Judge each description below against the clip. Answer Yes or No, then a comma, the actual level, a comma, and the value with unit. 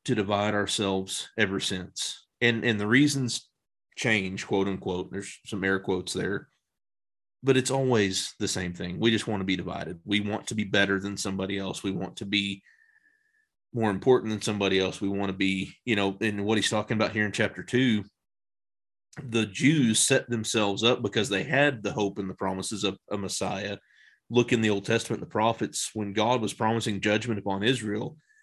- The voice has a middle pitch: No, low, 105 Hz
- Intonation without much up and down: No, average, 3.2 semitones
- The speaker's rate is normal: Yes, average, 190 wpm